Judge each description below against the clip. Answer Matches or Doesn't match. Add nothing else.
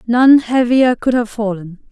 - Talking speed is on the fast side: Doesn't match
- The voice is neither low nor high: Doesn't match